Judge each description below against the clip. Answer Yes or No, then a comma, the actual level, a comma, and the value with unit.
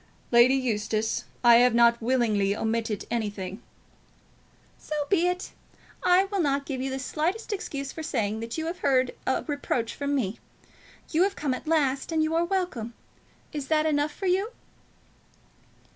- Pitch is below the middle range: No, very high, 270 Hz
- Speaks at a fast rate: No, average, 160 wpm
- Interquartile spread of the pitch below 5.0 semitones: No, wide, 5.5 semitones